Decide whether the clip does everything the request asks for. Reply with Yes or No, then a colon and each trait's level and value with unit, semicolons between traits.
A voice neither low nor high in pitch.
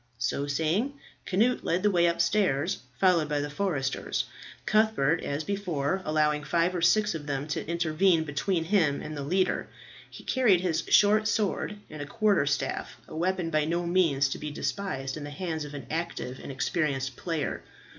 Yes: medium, 165 Hz